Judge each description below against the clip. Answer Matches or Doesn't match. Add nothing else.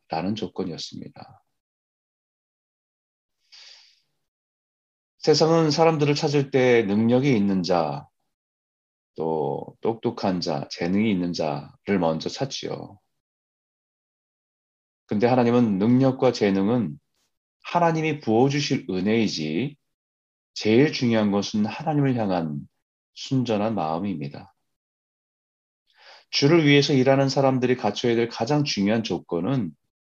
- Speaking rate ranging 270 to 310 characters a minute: Doesn't match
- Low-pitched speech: Matches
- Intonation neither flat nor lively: Doesn't match